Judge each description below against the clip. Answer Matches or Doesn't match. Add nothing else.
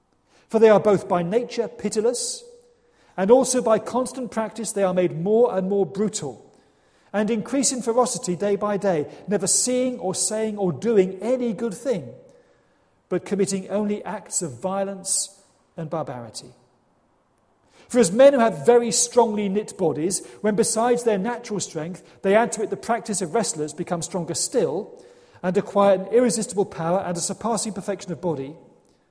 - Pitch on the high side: Matches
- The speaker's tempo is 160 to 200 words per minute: Matches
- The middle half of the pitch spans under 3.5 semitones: Doesn't match